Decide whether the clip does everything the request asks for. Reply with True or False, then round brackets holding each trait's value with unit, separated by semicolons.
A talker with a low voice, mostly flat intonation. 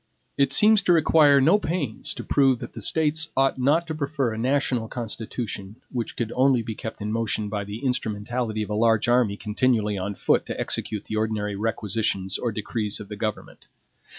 False (115 Hz; 4.4 semitones)